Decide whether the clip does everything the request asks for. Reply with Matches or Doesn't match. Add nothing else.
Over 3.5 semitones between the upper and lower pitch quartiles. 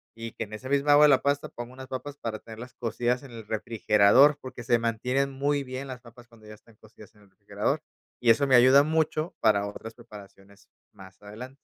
Matches